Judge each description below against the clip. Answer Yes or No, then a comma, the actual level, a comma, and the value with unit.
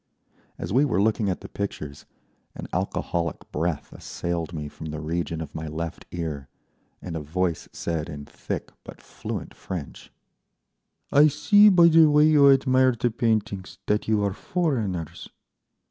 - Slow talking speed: No, average, 155 wpm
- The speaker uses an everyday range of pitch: No, wide, 8.2 semitones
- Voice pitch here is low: Yes, very low, 95 Hz